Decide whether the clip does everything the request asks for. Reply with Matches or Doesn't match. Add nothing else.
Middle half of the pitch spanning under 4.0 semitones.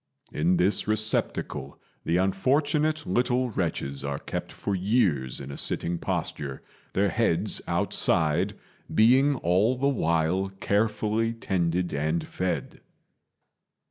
Doesn't match